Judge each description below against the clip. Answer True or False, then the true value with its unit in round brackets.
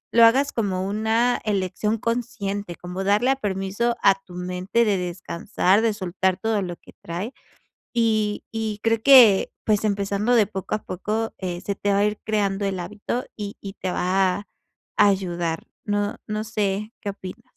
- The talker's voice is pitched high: True (205 Hz)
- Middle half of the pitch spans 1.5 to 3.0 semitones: True (2.7 semitones)